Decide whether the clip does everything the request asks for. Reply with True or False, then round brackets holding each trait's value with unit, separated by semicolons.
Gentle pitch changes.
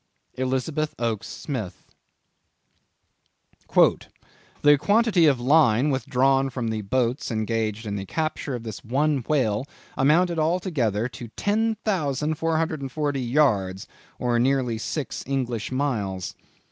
False (4.9 semitones)